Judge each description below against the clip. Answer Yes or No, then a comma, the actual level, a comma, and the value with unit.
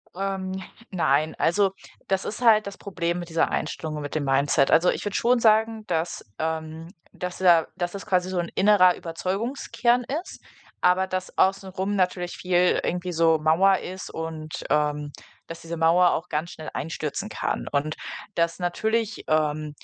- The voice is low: No, medium, 180 Hz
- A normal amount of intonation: Yes, average, 3.2 semitones